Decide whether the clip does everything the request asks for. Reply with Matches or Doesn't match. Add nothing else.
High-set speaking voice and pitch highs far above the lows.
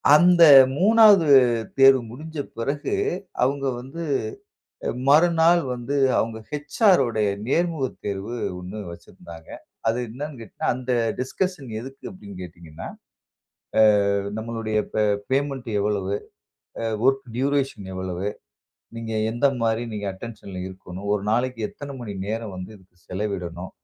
Doesn't match